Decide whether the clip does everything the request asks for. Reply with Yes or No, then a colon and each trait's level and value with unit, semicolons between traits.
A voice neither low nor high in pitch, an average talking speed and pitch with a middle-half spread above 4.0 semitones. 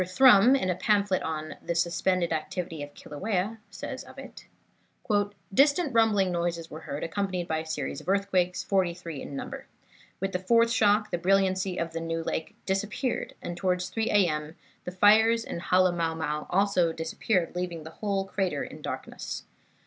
No: medium, 180 Hz; average, 165 wpm; average, 3.4 semitones